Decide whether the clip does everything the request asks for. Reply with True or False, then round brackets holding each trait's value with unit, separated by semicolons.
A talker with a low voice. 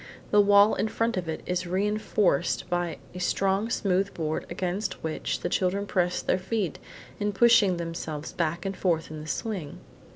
False (185 Hz)